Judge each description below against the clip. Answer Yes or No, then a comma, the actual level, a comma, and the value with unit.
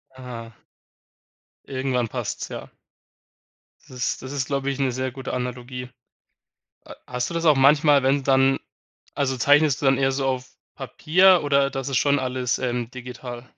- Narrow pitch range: Yes, narrow, 1.8 semitones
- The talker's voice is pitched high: No, low, 130 Hz